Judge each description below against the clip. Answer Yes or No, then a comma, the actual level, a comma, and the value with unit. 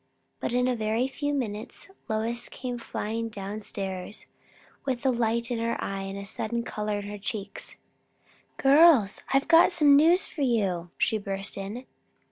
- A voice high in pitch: Yes, high, 225 Hz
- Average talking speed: Yes, average, 160 wpm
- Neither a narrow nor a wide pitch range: Yes, average, 3.8 semitones